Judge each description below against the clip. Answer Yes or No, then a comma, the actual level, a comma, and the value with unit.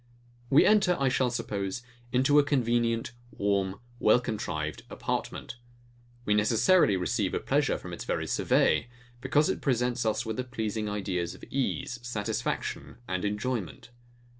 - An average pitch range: Yes, average, 3.6 semitones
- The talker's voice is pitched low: Yes, low, 115 Hz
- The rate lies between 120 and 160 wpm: Yes, average, 140 wpm